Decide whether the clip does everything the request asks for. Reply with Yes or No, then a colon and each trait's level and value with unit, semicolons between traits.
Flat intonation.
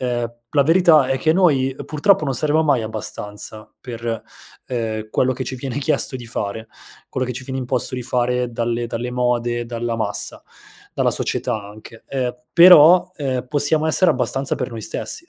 No: average, 3.3 semitones